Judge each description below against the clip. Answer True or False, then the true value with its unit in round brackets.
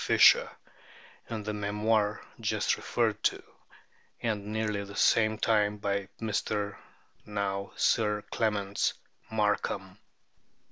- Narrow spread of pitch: True (1.2 semitones)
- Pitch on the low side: True (105 Hz)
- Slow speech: True (105 wpm)